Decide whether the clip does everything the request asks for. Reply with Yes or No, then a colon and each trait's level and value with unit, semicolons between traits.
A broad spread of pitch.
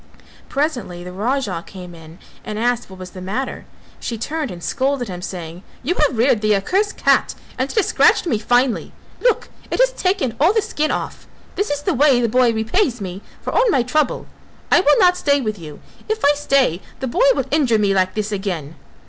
Yes: wide, 7.1 semitones